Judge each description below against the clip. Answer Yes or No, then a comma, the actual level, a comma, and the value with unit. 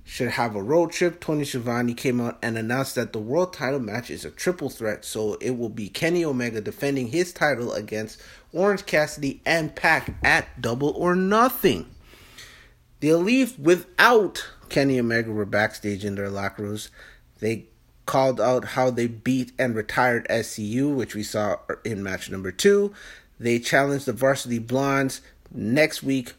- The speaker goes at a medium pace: Yes, average, 160 wpm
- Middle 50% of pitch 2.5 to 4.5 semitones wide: No, average, 5.3 semitones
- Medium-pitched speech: No, low, 125 Hz